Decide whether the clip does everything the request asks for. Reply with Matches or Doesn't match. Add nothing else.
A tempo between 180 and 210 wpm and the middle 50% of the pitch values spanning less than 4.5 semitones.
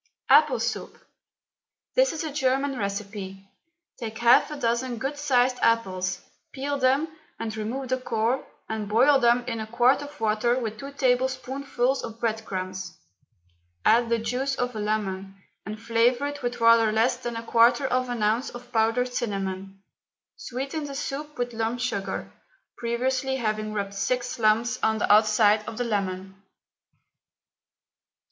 Doesn't match